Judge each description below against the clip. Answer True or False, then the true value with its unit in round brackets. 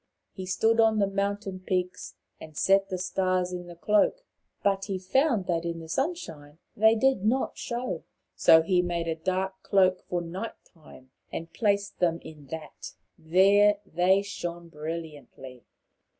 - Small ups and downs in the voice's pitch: False (3.3 semitones)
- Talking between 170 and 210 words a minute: False (155 wpm)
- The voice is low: False (185 Hz)